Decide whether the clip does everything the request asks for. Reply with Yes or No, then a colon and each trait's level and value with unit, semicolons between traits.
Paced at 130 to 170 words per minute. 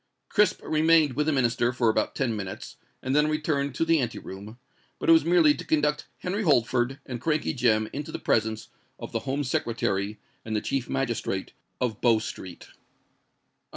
No: average, 180 wpm